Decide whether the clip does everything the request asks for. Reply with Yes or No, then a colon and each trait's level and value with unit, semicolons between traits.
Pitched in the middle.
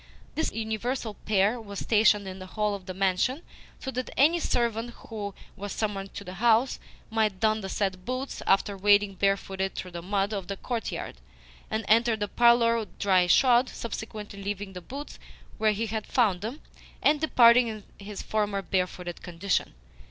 No: high, 210 Hz